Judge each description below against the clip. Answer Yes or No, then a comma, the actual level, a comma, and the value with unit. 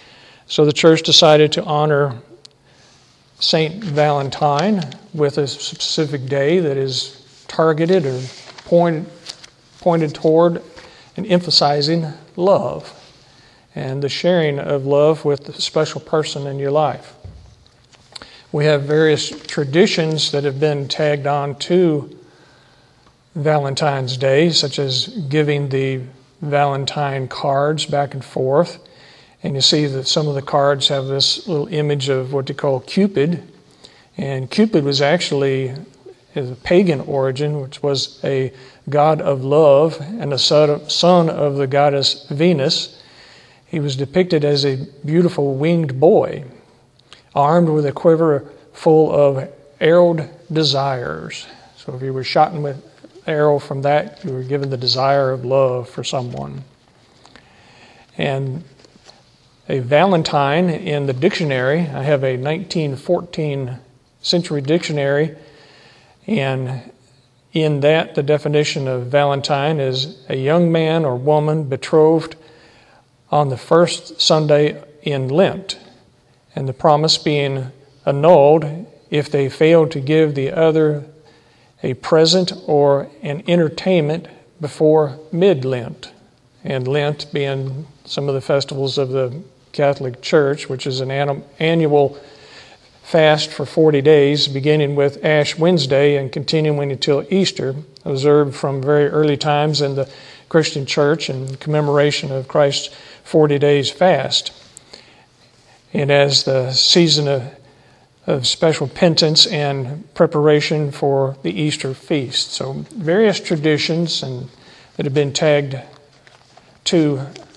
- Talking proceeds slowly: Yes, slow, 125 wpm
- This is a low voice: No, medium, 145 Hz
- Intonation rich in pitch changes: No, narrow, 2.5 semitones